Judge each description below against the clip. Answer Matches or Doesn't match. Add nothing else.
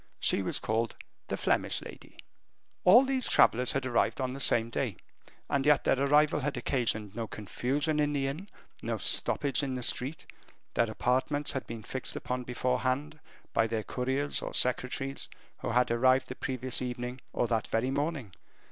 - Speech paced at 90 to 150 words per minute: Doesn't match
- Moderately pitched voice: Doesn't match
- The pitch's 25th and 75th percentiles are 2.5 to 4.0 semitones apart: Matches